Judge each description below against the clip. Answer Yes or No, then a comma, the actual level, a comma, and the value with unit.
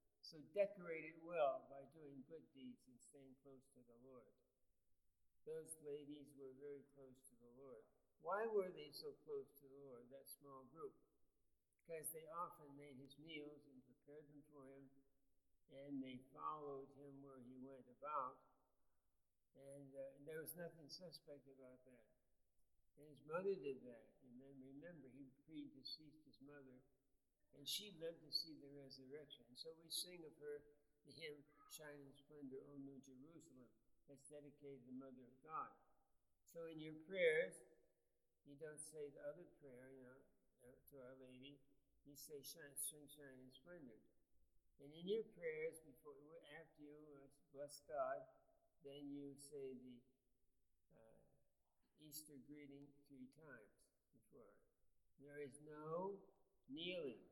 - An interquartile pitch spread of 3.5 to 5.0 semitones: No, narrow, 2.6 semitones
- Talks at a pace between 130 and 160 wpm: Yes, average, 155 wpm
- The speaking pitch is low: No, medium, 145 Hz